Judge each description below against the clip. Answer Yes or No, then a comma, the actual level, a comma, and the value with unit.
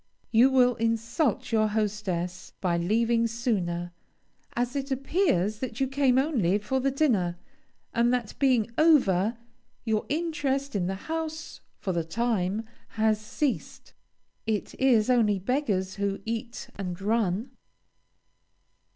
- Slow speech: Yes, slow, 125 wpm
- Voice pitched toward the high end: Yes, high, 230 Hz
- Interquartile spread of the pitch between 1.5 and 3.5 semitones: No, average, 4.9 semitones